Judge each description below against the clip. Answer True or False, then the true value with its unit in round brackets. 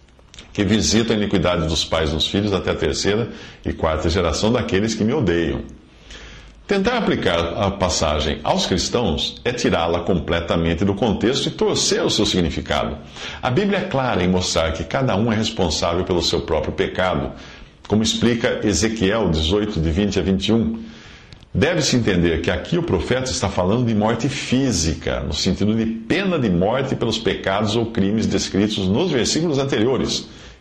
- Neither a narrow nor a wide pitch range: True (4.7 semitones)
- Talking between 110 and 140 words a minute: False (165 wpm)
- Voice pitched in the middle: False (95 Hz)